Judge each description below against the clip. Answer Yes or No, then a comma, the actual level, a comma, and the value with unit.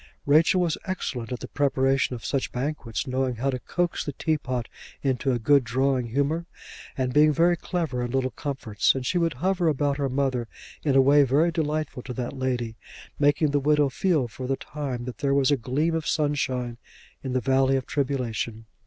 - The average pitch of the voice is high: No, low, 135 Hz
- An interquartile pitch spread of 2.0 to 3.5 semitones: Yes, average, 2.8 semitones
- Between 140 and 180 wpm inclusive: No, average, 195 wpm